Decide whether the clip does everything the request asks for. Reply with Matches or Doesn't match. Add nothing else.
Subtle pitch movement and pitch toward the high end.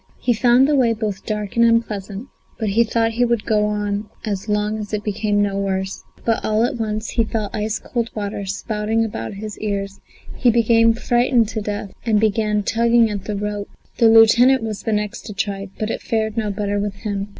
Matches